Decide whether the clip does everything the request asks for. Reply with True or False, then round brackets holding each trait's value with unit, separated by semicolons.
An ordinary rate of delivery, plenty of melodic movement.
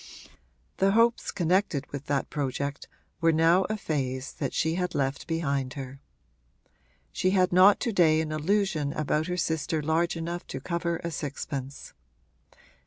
False (150 wpm; 4.1 semitones)